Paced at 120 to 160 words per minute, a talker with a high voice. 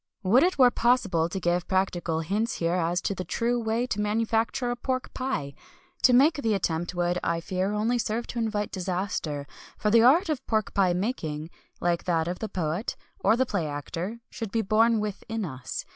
No: average, 195 wpm; high, 205 Hz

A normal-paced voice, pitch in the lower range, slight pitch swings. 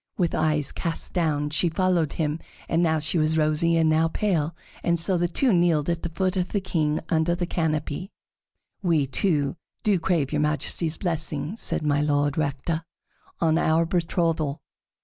No: average, 170 wpm; medium, 160 Hz; narrow, 2.2 semitones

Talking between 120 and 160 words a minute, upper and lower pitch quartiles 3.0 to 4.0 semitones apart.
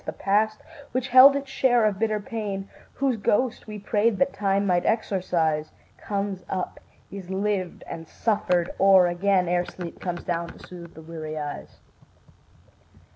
Yes: average, 155 wpm; average, 3.5 semitones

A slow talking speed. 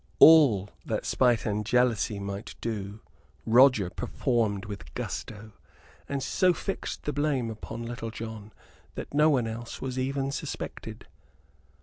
Yes: slow, 130 wpm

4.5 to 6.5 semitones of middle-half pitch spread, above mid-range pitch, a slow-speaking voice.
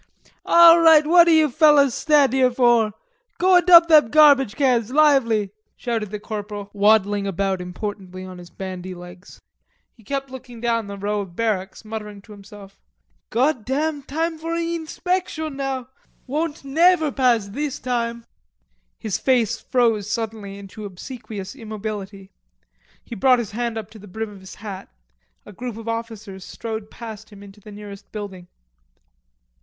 No: average, 5.2 semitones; high, 225 Hz; average, 155 wpm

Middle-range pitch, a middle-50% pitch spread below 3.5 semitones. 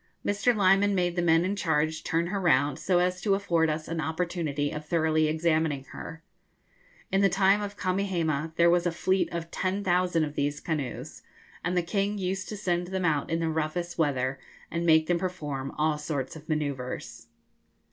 Yes: medium, 170 Hz; average, 3.0 semitones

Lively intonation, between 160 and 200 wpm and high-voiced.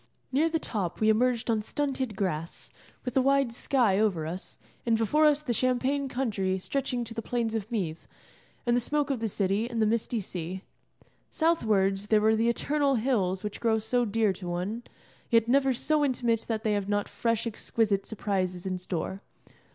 No: average, 4.1 semitones; average, 185 wpm; high, 225 Hz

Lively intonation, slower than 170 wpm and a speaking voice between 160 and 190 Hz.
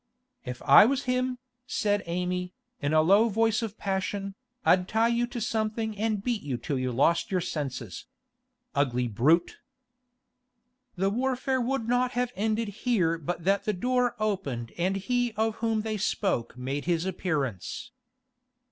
No: wide, 5.7 semitones; average, 155 wpm; high, 200 Hz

